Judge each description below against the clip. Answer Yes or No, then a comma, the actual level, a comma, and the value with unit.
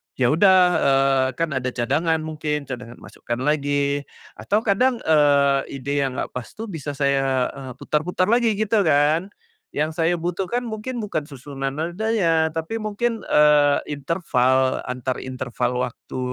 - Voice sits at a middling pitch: Yes, medium, 150 Hz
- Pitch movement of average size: Yes, average, 4.9 semitones